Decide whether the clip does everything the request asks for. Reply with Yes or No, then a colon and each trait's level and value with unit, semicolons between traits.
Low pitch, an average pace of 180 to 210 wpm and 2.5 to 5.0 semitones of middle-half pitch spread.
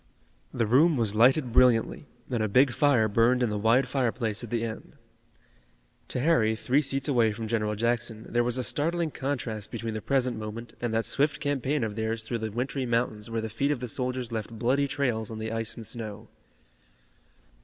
Yes: low, 120 Hz; average, 195 wpm; average, 2.8 semitones